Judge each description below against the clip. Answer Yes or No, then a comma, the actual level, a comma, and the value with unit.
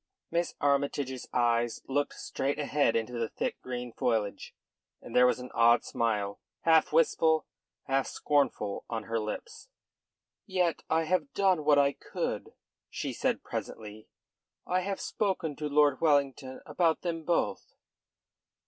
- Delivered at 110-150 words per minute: Yes, average, 140 wpm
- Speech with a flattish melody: No, average, 5.3 semitones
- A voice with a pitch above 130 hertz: Yes, medium, 140 Hz